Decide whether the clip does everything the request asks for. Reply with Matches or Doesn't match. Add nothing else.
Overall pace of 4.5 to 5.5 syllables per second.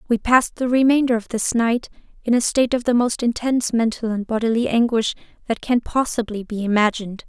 Doesn't match